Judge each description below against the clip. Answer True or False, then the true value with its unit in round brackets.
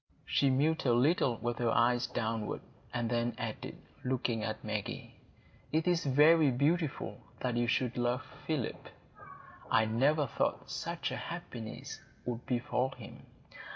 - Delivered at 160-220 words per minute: False (140 wpm)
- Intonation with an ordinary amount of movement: True (3.9 semitones)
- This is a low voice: True (125 Hz)